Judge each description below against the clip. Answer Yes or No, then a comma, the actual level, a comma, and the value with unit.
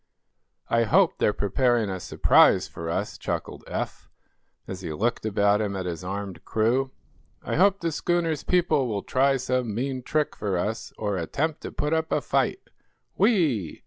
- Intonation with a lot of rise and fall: Yes, wide, 6.8 semitones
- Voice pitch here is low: Yes, low, 115 Hz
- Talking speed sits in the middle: Yes, average, 170 wpm